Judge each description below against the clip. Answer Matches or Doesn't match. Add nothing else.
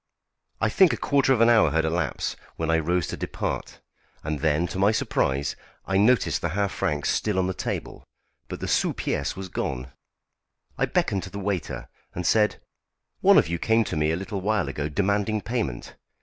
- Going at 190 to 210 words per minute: Matches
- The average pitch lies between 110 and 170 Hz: Doesn't match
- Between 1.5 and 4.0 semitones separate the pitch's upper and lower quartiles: Doesn't match